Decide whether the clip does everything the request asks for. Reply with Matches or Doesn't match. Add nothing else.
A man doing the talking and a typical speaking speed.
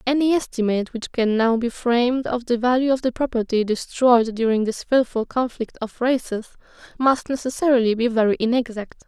Doesn't match